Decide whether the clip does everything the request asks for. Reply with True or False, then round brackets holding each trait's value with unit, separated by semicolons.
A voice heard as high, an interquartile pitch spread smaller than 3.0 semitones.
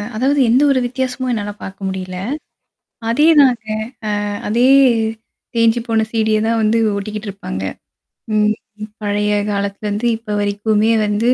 True (220 Hz; 2.6 semitones)